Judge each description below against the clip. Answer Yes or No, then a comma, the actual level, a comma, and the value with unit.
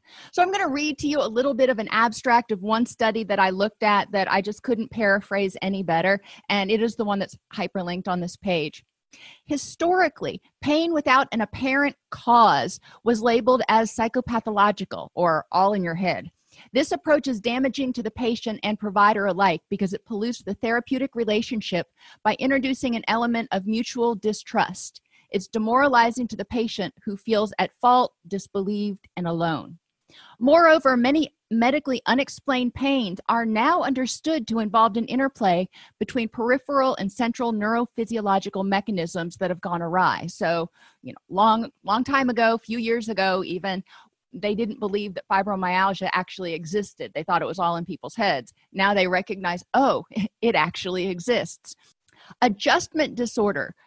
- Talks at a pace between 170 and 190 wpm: No, average, 160 wpm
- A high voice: Yes, high, 220 Hz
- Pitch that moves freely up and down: No, average, 4.1 semitones